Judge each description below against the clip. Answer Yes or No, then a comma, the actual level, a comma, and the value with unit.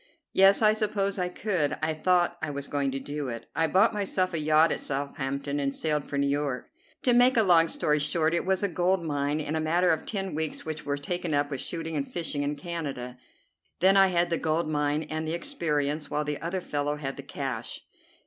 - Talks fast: Yes, fast, 225 wpm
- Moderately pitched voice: Yes, medium, 155 Hz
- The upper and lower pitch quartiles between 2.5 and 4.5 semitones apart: Yes, average, 3.7 semitones